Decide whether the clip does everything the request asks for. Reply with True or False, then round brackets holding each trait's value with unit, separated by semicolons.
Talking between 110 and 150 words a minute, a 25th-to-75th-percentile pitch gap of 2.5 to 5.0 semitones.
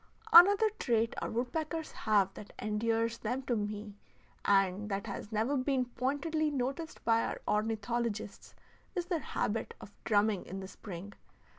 True (145 wpm; 4.5 semitones)